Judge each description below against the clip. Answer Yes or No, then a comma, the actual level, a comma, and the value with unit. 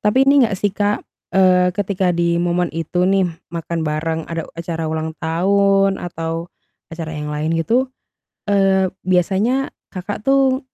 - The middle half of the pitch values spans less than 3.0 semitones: No, average, 3.4 semitones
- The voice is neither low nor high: Yes, medium, 180 Hz